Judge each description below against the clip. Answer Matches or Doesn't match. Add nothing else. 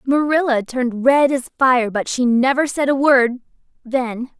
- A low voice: Doesn't match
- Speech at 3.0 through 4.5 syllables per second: Matches